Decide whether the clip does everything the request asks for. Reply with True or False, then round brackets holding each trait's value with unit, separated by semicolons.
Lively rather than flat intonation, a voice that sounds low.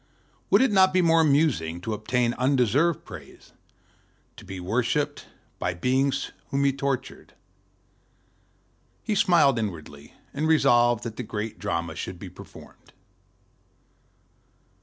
True (6.0 semitones; 125 Hz)